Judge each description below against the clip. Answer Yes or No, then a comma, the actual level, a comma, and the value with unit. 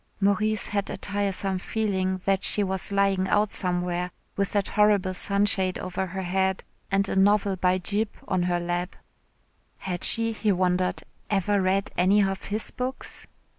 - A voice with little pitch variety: Yes, narrow, 1.6 semitones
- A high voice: Yes, high, 195 Hz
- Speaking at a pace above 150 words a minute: Yes, average, 160 wpm